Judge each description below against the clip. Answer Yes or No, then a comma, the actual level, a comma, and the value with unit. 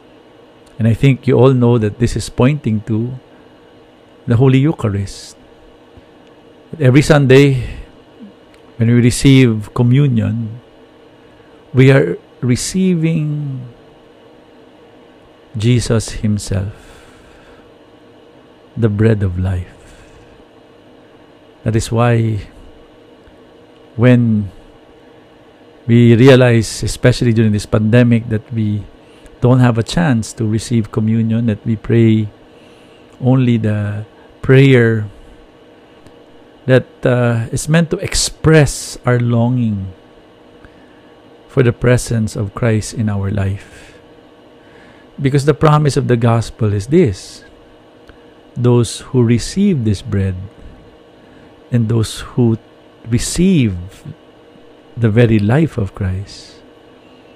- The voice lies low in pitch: Yes, low, 115 Hz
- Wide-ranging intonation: No, average, 3.3 semitones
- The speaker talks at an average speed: No, slow, 95 wpm